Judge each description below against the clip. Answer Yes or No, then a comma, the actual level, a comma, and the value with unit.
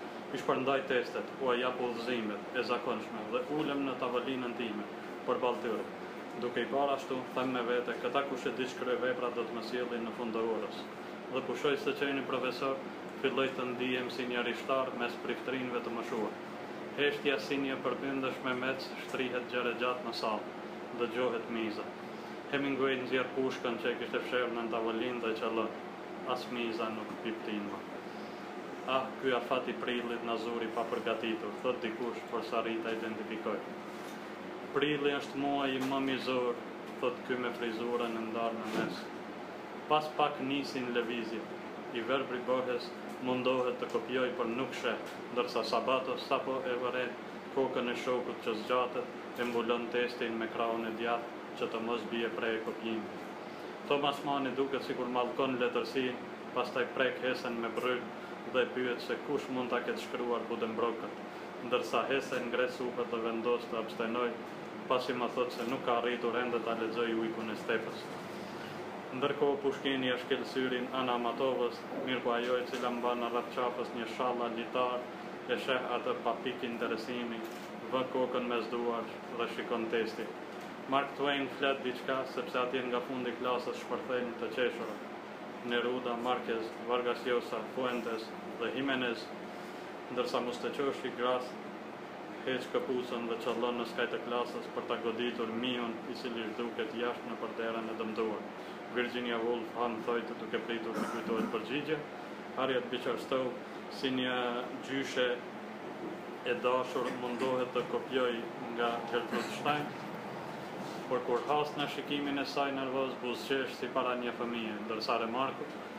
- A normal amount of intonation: No, narrow, 1.5 semitones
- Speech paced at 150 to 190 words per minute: Yes, average, 155 wpm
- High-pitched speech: No, low, 120 Hz